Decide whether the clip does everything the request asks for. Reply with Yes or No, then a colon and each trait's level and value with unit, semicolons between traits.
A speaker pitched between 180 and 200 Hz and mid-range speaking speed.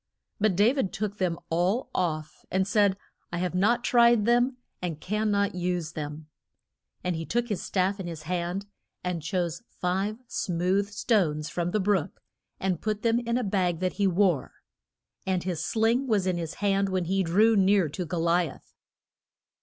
Yes: high, 190 Hz; average, 180 wpm